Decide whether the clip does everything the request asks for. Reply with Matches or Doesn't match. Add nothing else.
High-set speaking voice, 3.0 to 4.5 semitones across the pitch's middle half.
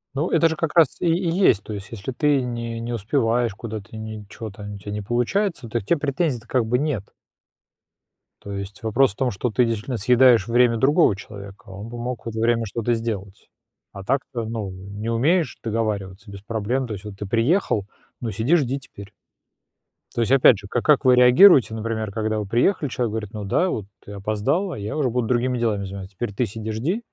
Doesn't match